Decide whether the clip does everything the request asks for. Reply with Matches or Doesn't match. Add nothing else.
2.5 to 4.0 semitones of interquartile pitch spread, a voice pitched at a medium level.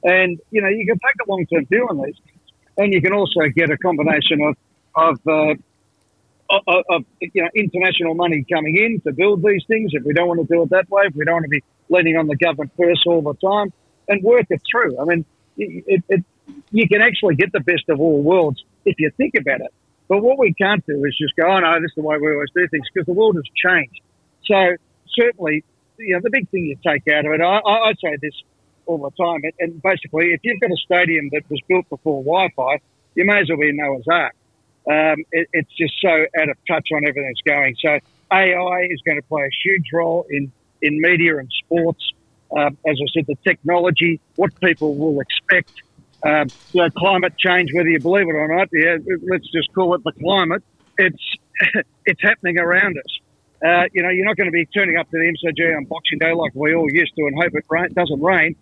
Matches